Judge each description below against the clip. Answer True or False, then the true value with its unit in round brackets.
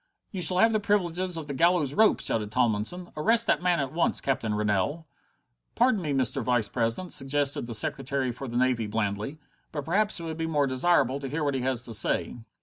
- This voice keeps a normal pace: False (210 wpm)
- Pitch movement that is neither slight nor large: False (6.1 semitones)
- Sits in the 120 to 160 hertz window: True (140 Hz)